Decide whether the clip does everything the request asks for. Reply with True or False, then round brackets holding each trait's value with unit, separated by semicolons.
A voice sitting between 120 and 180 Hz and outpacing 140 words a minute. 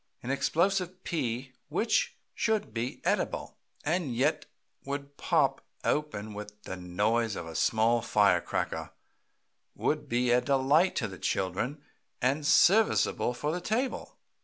False (135 Hz; 135 wpm)